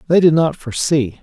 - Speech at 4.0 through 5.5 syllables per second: No, 5.8 syllables/s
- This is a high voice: No, medium, 150 Hz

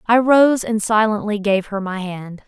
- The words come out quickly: No, average, 195 wpm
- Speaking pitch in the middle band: No, high, 210 Hz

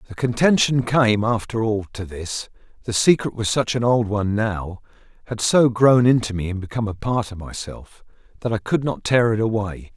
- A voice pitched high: No, low, 110 Hz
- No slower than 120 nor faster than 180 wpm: No, average, 195 wpm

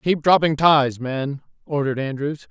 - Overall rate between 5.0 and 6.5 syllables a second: No, 4.6 syllables/s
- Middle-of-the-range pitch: Yes, medium, 145 Hz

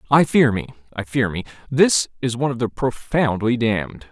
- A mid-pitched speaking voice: No, low, 120 Hz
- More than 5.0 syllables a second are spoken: Yes, 5.2 syllables/s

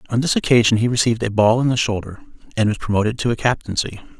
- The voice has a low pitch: Yes, low, 115 Hz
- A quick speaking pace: Yes, fast, 230 wpm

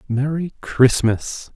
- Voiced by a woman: No, male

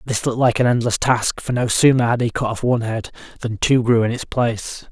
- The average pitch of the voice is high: No, low, 120 Hz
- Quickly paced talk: Yes, fast, 270 wpm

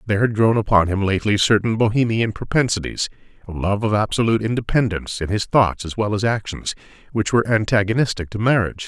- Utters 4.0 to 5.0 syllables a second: No, 6.4 syllables/s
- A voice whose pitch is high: No, low, 105 Hz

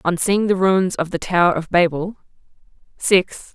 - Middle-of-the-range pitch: Yes, medium, 180 Hz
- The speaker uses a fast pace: No, average, 170 wpm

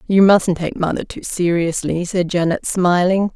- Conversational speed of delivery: Yes, average, 160 wpm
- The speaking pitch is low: No, medium, 180 Hz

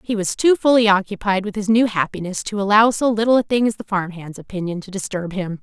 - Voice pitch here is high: Yes, high, 205 Hz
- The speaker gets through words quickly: Yes, fast, 245 wpm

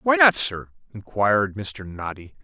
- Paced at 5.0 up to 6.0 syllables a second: No, 4.2 syllables/s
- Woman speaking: No, male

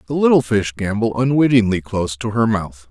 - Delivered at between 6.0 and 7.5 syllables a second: No, 5.5 syllables/s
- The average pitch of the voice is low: Yes, low, 110 Hz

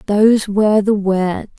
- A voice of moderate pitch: No, high, 205 Hz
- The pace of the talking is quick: No, average, 150 wpm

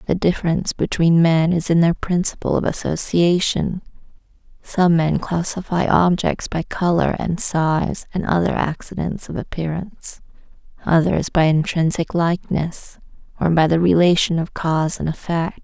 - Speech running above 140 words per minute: No, slow, 135 wpm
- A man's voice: No, female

